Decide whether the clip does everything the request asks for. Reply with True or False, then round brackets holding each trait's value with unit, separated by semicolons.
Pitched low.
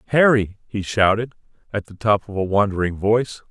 True (105 Hz)